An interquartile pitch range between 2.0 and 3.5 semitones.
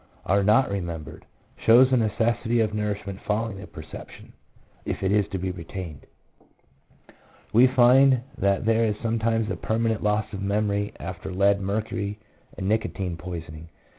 Yes: average, 2.8 semitones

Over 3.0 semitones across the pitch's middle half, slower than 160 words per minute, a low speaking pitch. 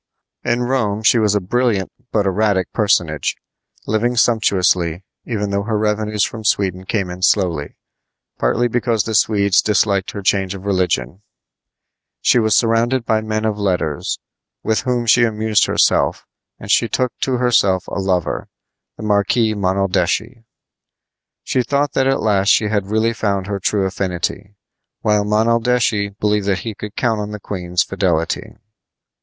No: average, 2.7 semitones; average, 150 wpm; low, 105 Hz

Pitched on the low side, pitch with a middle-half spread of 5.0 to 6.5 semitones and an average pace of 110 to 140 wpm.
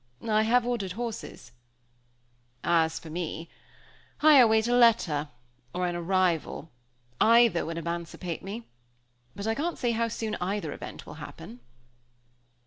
No: high, 200 Hz; wide, 5.5 semitones; slow, 135 wpm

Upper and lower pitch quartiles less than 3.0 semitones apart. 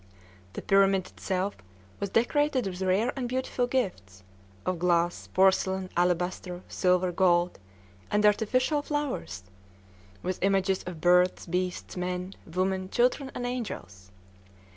No: average, 3.8 semitones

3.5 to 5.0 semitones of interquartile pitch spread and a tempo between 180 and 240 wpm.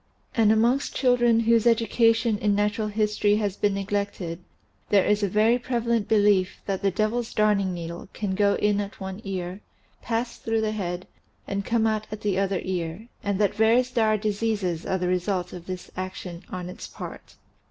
No: average, 2.8 semitones; average, 185 wpm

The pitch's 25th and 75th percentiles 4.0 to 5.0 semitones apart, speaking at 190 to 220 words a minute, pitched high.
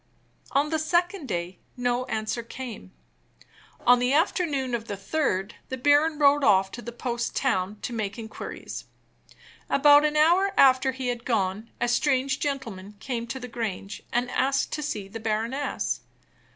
No: average, 4.5 semitones; average, 160 wpm; high, 245 Hz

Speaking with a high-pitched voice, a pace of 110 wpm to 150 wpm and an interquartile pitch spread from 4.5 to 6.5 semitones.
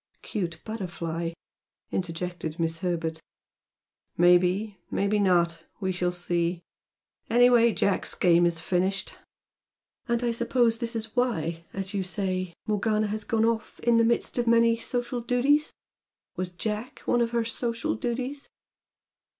Yes: high, 205 Hz; slow, 135 wpm; average, 4.8 semitones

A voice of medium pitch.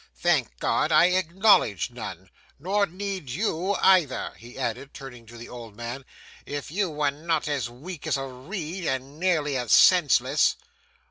Yes: medium, 145 Hz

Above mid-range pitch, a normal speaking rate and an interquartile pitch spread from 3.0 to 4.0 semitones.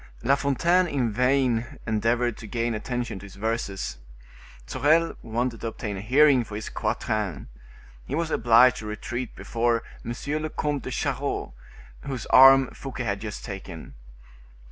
No: low, 120 Hz; average, 150 wpm; average, 3.7 semitones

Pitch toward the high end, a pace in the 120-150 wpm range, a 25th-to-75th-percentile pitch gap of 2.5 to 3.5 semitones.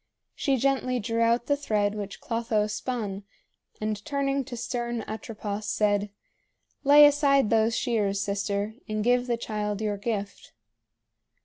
Yes: high, 225 Hz; slow, 135 wpm; average, 3.1 semitones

